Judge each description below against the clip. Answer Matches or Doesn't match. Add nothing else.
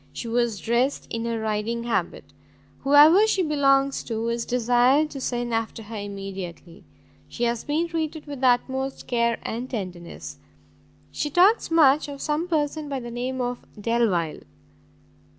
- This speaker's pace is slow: Doesn't match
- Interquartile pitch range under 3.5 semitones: Doesn't match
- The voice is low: Doesn't match